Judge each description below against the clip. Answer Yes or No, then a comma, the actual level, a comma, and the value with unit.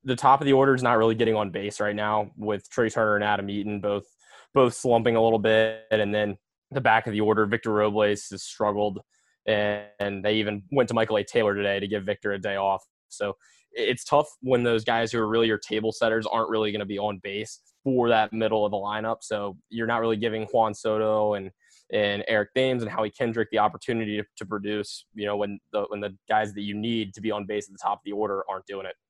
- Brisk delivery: Yes, fast, 245 wpm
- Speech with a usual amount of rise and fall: No, narrow, 1.6 semitones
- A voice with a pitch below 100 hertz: No, low, 105 Hz